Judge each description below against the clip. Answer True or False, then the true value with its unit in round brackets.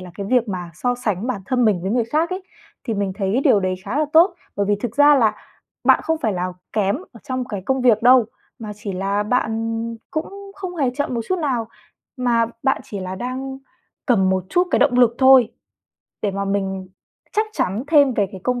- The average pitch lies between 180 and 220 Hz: False (230 Hz)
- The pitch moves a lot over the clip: False (4.8 semitones)